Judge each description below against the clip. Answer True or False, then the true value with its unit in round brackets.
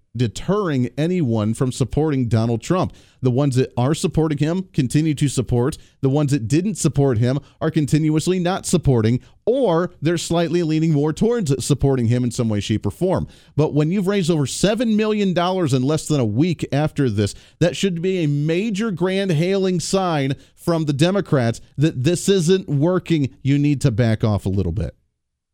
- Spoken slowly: False (180 wpm)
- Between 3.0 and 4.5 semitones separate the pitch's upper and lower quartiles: False (5.2 semitones)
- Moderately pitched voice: True (150 Hz)